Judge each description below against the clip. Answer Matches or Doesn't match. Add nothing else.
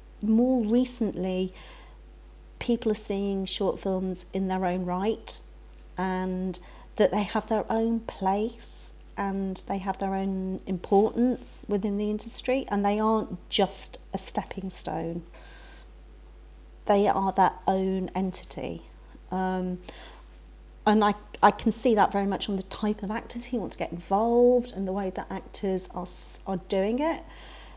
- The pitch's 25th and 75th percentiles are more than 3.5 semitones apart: Doesn't match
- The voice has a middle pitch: Doesn't match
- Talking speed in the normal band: Matches